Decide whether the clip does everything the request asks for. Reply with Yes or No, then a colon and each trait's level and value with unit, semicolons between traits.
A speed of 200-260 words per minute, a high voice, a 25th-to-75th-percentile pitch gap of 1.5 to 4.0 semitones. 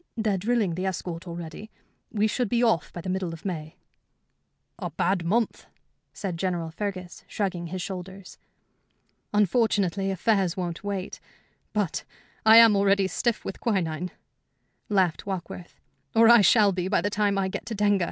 No: average, 155 wpm; high, 195 Hz; average, 2.7 semitones